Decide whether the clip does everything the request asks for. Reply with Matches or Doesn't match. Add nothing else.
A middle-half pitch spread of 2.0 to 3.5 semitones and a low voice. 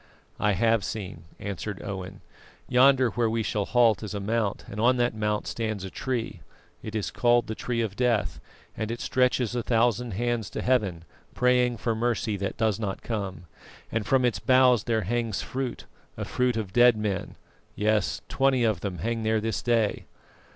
Matches